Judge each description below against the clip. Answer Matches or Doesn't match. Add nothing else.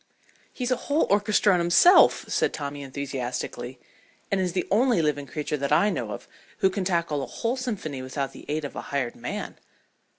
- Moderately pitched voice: Matches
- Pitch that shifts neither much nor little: Doesn't match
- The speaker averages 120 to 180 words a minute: Doesn't match